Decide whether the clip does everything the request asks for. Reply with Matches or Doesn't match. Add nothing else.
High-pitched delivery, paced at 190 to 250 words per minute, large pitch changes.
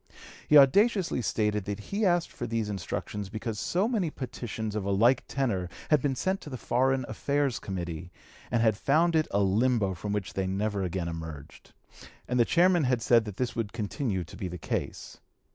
Doesn't match